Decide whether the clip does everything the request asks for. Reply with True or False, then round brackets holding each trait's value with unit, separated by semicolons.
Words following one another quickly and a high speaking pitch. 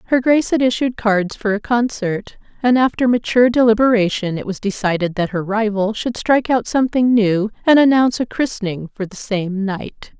False (180 wpm; 220 Hz)